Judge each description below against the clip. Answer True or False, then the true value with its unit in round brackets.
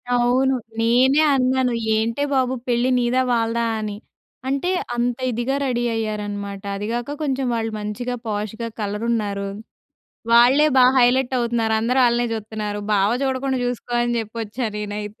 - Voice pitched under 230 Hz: False (235 Hz)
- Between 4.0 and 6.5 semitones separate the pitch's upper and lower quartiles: False (2.9 semitones)